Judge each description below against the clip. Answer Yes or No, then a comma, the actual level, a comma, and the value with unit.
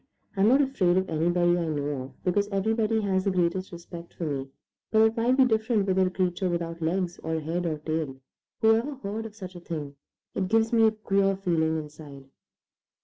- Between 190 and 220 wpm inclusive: Yes, average, 200 wpm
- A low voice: No, medium, 185 Hz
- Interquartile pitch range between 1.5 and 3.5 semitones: No, average, 4.6 semitones